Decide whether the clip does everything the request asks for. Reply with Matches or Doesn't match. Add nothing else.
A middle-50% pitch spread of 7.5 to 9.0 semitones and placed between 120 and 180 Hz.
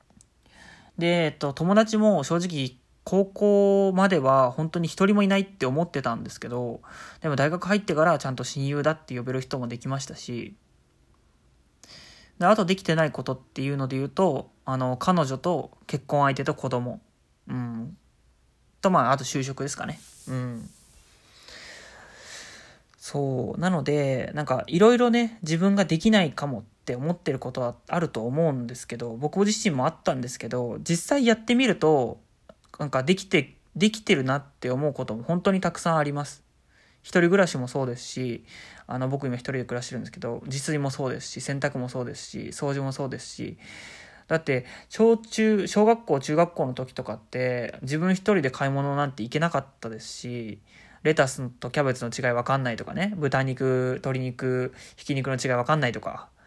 Doesn't match